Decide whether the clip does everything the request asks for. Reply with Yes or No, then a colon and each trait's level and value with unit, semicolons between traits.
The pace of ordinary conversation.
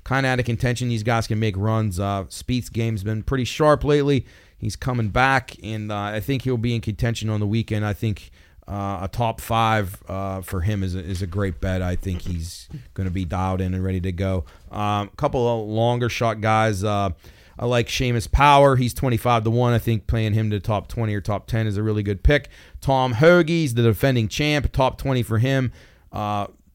No: fast, 225 wpm